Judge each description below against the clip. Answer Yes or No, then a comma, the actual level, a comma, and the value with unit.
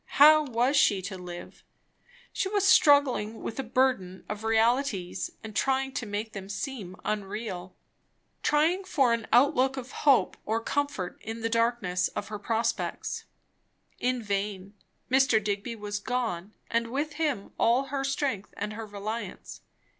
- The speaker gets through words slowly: No, average, 145 wpm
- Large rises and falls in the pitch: No, average, 4.5 semitones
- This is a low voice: No, high, 230 Hz